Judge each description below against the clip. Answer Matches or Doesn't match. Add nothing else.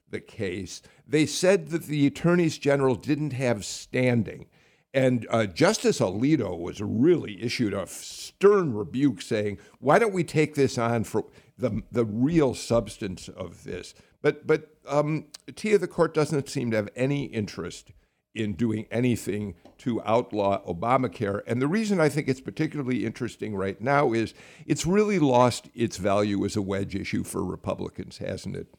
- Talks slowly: Doesn't match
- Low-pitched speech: Matches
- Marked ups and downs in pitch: Matches